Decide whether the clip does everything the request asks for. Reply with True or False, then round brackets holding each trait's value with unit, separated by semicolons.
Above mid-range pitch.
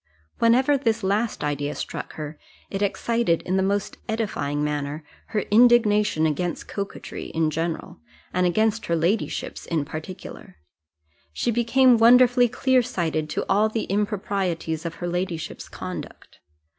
True (195 Hz)